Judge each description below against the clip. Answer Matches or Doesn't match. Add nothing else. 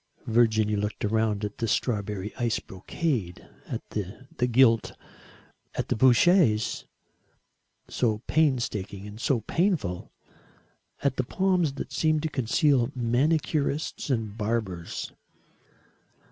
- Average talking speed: Doesn't match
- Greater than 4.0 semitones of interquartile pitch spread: Matches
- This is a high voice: Doesn't match